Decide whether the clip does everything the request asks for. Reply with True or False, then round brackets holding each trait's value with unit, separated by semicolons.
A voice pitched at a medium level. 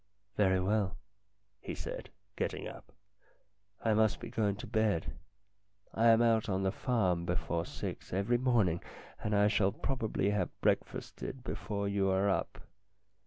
False (105 Hz)